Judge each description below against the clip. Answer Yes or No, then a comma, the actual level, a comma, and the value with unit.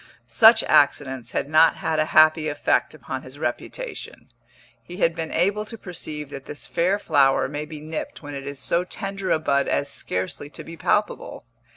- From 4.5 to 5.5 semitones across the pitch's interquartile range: No, average, 3.9 semitones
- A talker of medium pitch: Yes, medium, 155 Hz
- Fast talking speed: No, average, 185 wpm